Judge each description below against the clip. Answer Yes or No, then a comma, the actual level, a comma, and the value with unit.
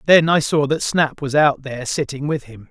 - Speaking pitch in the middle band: Yes, medium, 145 Hz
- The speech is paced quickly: Yes, fast, 245 wpm